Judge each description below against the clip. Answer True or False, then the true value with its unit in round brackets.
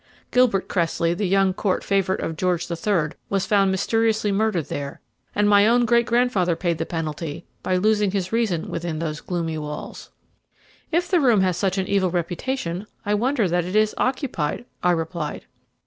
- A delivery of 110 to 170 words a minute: False (180 wpm)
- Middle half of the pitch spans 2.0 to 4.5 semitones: True (4.1 semitones)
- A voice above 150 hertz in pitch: True (190 Hz)